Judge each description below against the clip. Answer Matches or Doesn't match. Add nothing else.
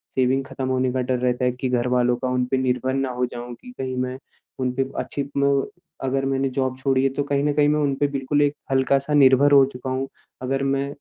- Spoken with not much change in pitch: Matches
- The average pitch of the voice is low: Matches